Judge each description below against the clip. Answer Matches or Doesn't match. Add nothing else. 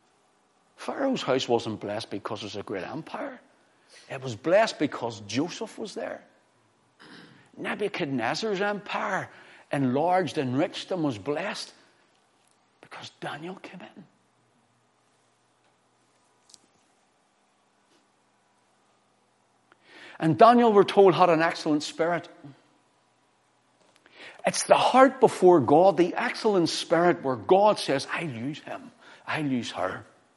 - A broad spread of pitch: Matches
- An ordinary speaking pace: Doesn't match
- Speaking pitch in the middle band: Matches